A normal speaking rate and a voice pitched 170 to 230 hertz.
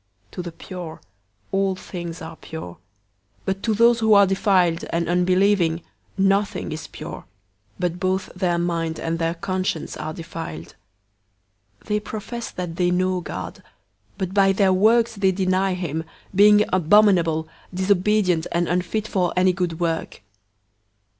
Yes: average, 145 wpm; medium, 185 Hz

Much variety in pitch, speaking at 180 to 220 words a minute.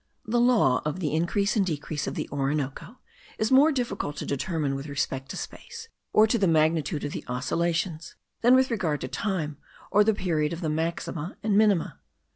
Yes: wide, 6.1 semitones; average, 190 wpm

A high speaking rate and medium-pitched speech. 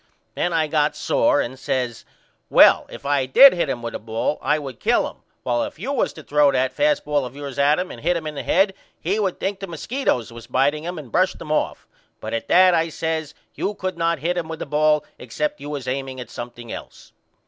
Yes: fast, 245 wpm; medium, 150 Hz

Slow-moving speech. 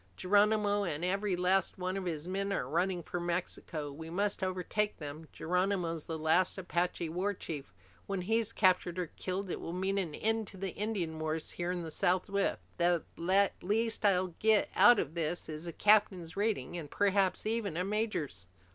No: average, 175 wpm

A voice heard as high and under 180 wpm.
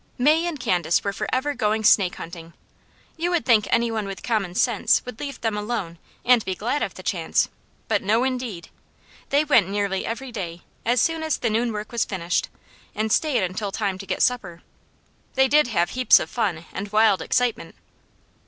No: high, 220 Hz; average, 190 wpm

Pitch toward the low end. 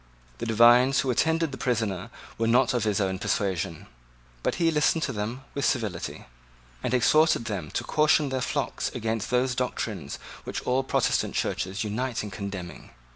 Yes: low, 115 Hz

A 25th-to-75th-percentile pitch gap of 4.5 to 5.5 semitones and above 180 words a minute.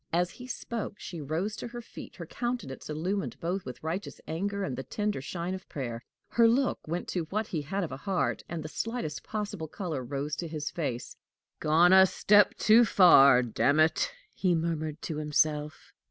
Yes: average, 5.1 semitones; average, 190 wpm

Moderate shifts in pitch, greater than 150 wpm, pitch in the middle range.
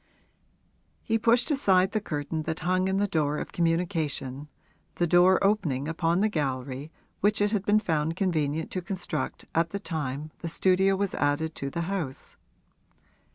Yes: average, 4.4 semitones; average, 160 wpm; medium, 170 Hz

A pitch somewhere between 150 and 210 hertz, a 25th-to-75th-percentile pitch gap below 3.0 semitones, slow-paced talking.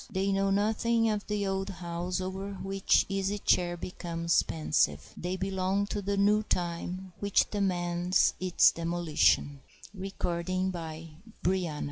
Yes: high, 190 Hz; narrow, 2.4 semitones; slow, 125 wpm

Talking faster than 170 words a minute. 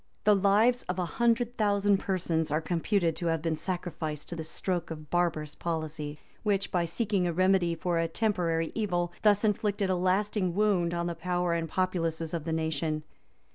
Yes: average, 180 wpm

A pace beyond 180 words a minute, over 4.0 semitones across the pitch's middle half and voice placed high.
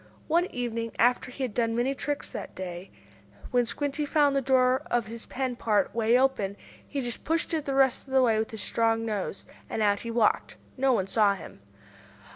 No: fast, 205 wpm; average, 3.3 semitones; high, 240 Hz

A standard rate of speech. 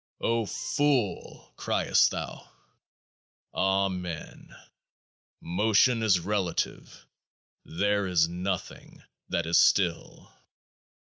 No: slow, 70 wpm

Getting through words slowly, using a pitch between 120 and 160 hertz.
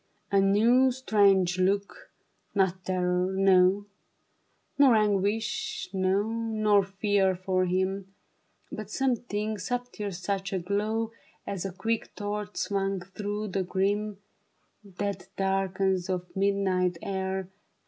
No: slow, 115 wpm; high, 195 Hz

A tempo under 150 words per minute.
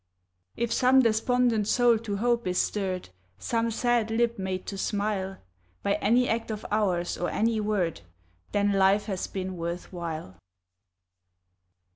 Yes: average, 140 wpm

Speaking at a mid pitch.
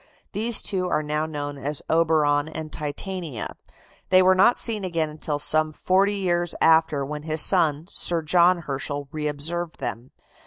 Yes: medium, 160 Hz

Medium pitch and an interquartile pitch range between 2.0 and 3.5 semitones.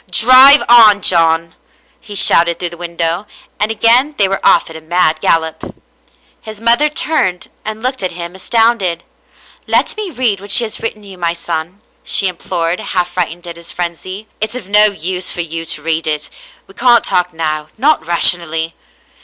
No: medium, 180 Hz; average, 4.5 semitones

